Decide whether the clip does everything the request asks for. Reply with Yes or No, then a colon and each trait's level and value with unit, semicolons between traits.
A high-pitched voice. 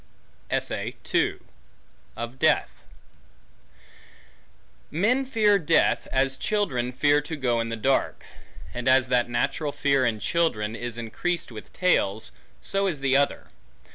No: low, 135 Hz